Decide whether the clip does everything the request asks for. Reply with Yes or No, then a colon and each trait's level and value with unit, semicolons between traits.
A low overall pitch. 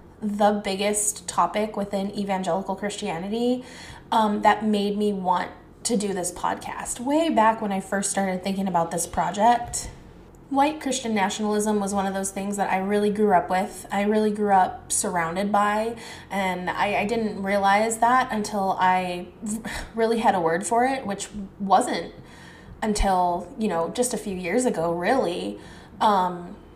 No: high, 205 Hz